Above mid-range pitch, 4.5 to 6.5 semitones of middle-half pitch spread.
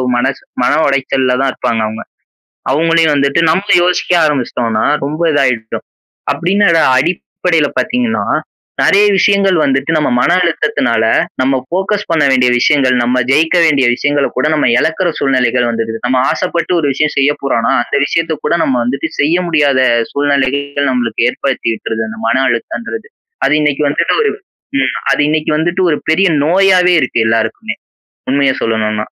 No: medium, 140 Hz; average, 4.8 semitones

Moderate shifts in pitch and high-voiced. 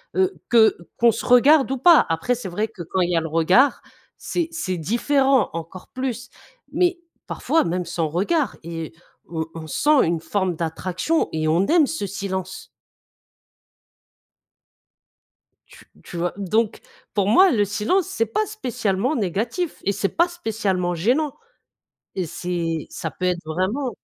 No: wide, 7.5 semitones; high, 205 Hz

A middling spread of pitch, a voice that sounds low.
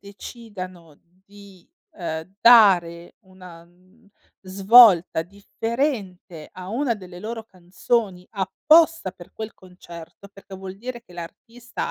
No: average, 3.8 semitones; high, 190 Hz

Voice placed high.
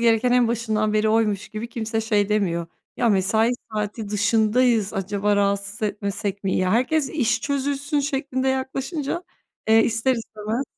Yes: high, 220 Hz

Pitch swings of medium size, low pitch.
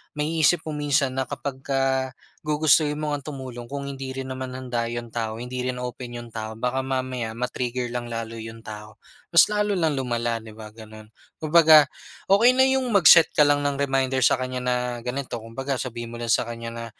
Yes: average, 3.5 semitones; low, 130 Hz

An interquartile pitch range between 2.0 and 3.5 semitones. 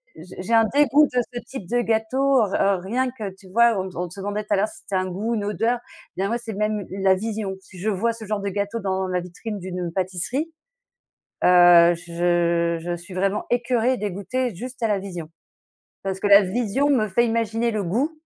No: average, 4.0 semitones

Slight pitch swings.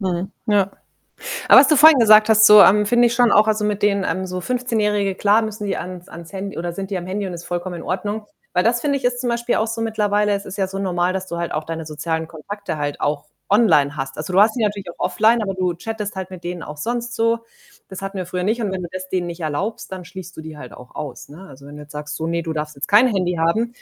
No: average, 3.9 semitones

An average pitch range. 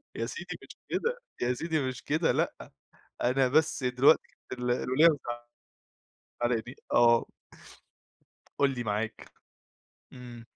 Yes: average, 3.3 semitones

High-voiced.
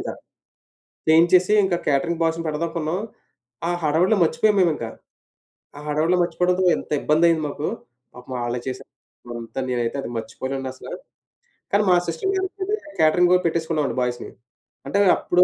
No: medium, 160 Hz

